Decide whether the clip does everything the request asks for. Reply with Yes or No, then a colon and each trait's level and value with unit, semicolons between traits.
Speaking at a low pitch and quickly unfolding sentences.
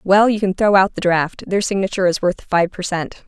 No: high, 190 Hz; fast, 255 wpm